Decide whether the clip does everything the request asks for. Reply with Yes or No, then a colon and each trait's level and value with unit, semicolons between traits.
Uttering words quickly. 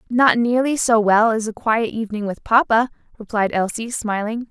No: average, 175 wpm